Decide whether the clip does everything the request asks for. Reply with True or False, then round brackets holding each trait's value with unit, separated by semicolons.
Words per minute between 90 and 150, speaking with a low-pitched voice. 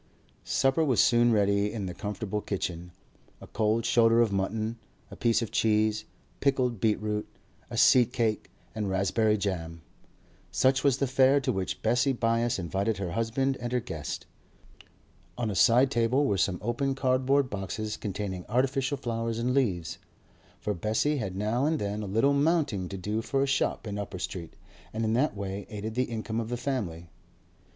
False (175 wpm; 110 Hz)